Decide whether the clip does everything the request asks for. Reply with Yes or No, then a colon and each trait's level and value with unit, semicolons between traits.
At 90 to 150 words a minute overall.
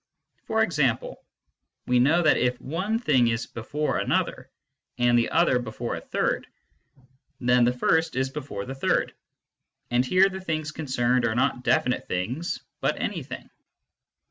Yes: average, 145 wpm